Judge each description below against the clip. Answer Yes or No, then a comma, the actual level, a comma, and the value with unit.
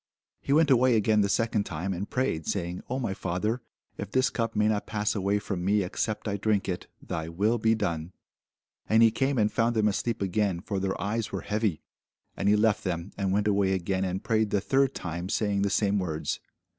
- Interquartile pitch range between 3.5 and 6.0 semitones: No, average, 2.8 semitones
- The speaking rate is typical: No, fast, 215 wpm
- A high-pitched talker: No, low, 105 Hz